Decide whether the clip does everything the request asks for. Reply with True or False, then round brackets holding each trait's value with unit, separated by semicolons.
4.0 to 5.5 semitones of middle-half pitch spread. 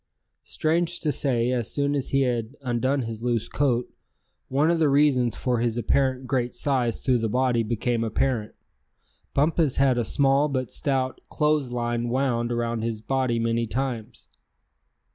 False (2.7 semitones)